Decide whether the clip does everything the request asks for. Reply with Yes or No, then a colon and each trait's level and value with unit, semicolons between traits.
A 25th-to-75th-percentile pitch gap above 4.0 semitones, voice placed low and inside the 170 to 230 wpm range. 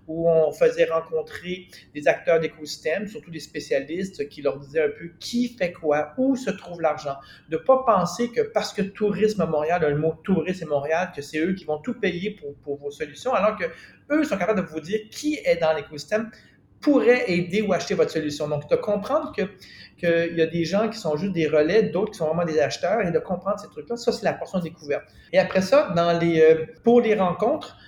No: average, 5.2 semitones; medium, 175 Hz; fast, 220 wpm